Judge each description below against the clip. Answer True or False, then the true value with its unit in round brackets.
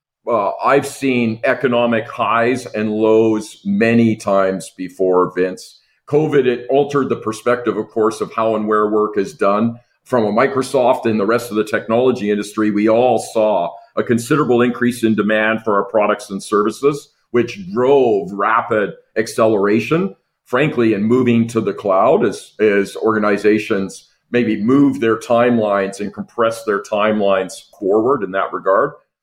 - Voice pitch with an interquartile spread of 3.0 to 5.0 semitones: False (2.5 semitones)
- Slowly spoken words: False (150 wpm)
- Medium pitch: False (110 Hz)